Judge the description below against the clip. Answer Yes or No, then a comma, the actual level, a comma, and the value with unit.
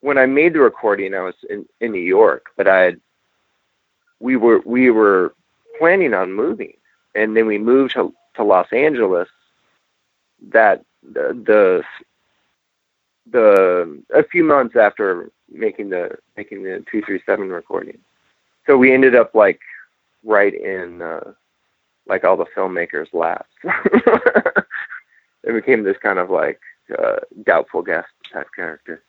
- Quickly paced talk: No, average, 140 wpm